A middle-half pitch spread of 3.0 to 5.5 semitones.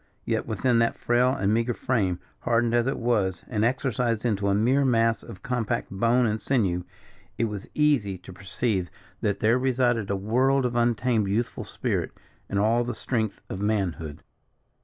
Yes: average, 3.4 semitones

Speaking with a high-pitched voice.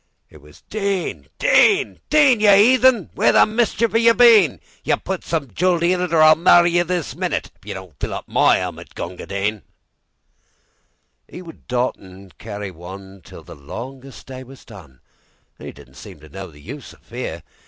No: low, 130 Hz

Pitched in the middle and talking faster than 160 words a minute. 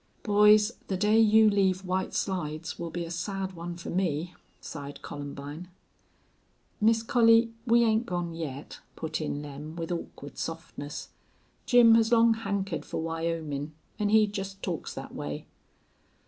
No: medium, 180 Hz; average, 150 wpm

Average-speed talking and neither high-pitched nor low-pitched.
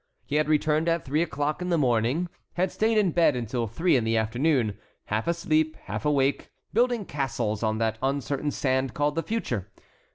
Yes: average, 185 wpm; medium, 145 Hz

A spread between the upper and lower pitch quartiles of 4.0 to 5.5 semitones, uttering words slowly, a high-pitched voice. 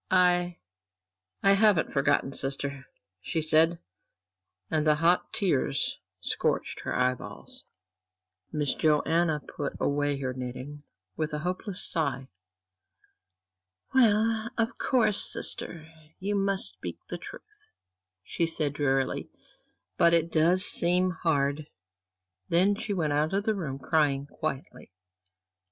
No: average, 4.4 semitones; slow, 115 wpm; medium, 160 Hz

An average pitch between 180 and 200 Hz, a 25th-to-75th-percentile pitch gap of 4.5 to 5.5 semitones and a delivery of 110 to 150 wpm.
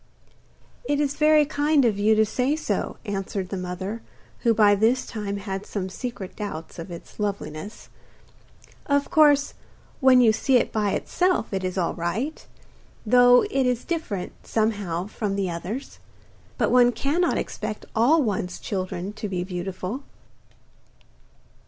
No: high, 215 Hz; average, 5.2 semitones; average, 145 wpm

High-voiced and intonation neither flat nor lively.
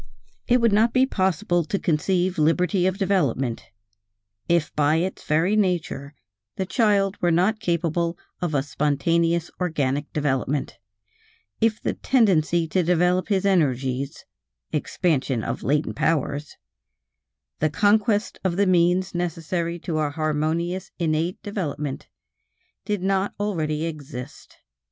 No: medium, 170 Hz; average, 3.9 semitones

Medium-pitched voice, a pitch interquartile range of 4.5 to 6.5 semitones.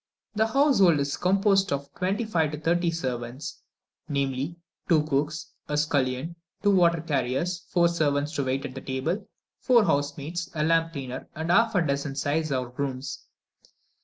No: medium, 155 Hz; average, 3.9 semitones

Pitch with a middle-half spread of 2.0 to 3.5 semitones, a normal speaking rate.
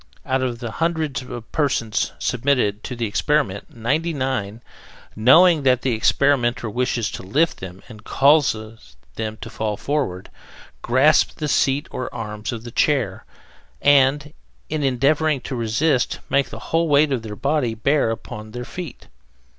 No: average, 4.6 semitones; average, 150 wpm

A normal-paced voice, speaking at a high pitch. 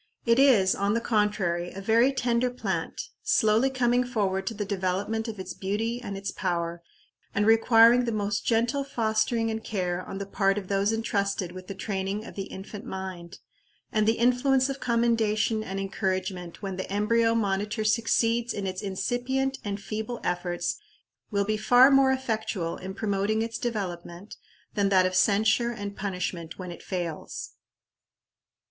Yes: average, 165 wpm; high, 210 Hz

